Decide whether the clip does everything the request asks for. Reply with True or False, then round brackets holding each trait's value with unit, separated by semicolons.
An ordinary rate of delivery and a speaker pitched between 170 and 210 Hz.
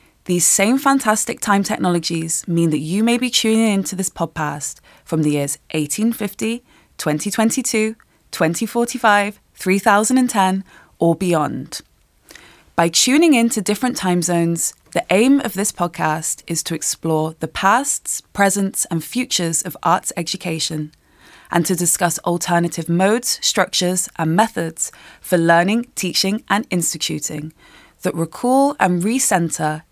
False (125 wpm; 185 Hz)